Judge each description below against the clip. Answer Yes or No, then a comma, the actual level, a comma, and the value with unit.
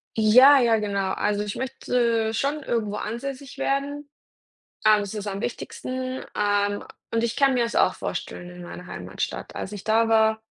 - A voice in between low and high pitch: No, high, 225 Hz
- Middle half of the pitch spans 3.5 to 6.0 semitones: Yes, average, 3.9 semitones